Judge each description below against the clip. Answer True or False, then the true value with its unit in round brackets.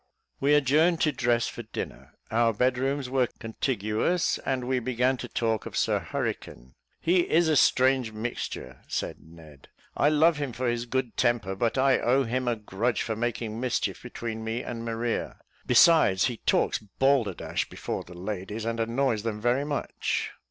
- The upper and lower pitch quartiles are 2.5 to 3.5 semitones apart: True (3.1 semitones)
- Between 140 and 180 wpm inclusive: True (170 wpm)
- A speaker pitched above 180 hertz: False (120 Hz)